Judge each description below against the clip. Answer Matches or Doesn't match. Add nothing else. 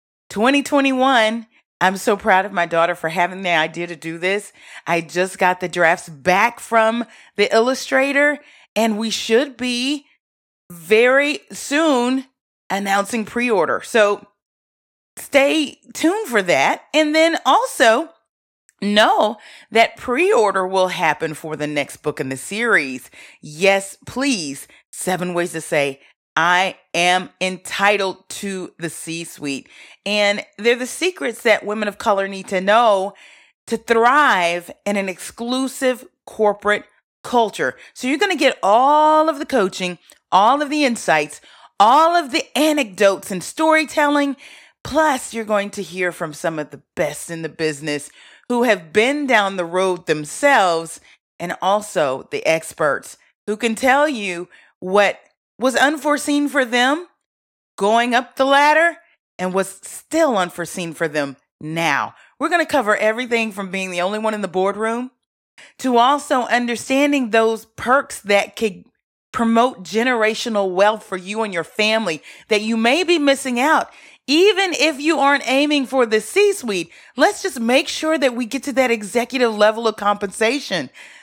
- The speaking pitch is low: Doesn't match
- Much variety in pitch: Matches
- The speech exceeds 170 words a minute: Doesn't match